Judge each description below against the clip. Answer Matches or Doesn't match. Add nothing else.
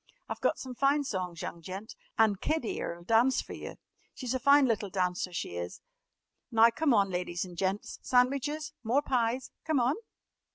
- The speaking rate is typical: Matches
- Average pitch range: Doesn't match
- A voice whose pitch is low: Doesn't match